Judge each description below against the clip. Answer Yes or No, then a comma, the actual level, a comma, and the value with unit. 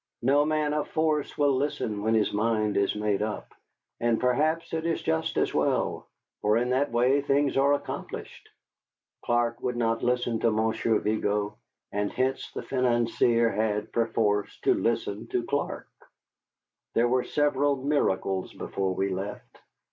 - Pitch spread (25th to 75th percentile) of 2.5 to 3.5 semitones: No, average, 4.5 semitones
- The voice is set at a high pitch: No, low, 120 Hz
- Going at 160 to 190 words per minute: No, average, 150 wpm